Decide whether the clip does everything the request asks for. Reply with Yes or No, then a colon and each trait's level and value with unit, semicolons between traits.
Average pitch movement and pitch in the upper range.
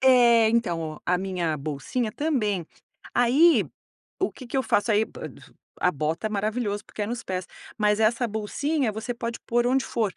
Yes: average, 4.1 semitones; high, 220 Hz